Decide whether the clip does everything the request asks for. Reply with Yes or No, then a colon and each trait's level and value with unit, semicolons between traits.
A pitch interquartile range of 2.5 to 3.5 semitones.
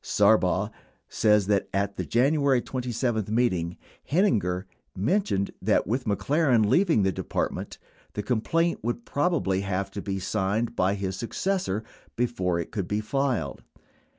No: average, 5.0 semitones